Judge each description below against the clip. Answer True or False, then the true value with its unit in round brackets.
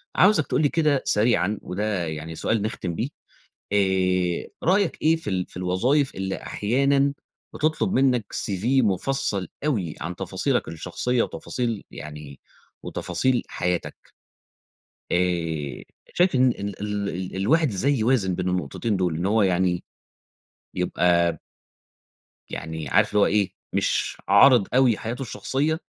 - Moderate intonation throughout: False (6.3 semitones)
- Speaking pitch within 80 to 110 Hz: True (105 Hz)